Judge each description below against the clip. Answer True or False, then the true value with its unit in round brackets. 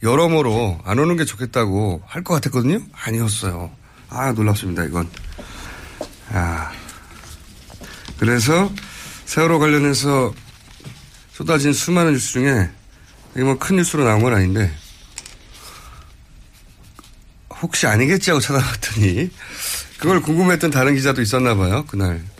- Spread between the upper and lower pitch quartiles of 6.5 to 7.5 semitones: True (7.0 semitones)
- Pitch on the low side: True (120 Hz)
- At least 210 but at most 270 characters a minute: True (255 characters per minute)